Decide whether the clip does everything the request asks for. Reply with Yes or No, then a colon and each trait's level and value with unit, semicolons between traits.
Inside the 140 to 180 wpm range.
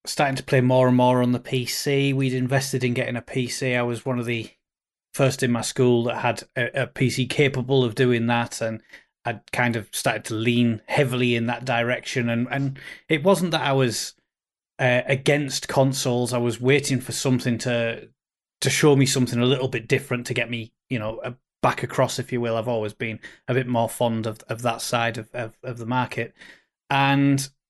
No: fast, 205 wpm